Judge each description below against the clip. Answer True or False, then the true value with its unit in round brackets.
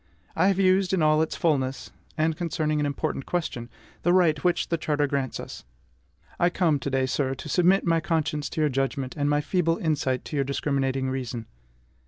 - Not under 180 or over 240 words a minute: True (195 wpm)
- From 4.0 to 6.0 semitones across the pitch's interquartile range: False (3.6 semitones)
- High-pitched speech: False (150 Hz)